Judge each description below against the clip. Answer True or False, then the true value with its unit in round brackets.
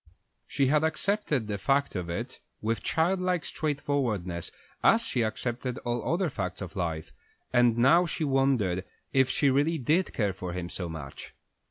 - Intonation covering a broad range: True (8.1 semitones)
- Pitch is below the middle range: True (125 Hz)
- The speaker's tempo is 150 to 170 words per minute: True (160 wpm)